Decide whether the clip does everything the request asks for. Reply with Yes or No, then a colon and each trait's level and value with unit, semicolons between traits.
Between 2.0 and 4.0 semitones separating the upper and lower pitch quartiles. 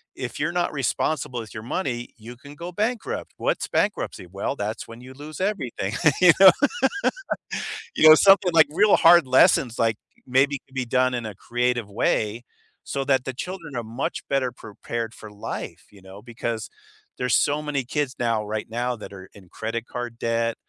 No: average, 4.4 semitones